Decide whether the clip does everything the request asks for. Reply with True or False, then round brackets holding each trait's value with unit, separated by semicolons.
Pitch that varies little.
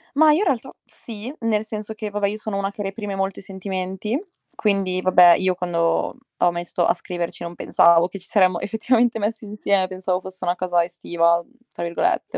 False (3.1 semitones)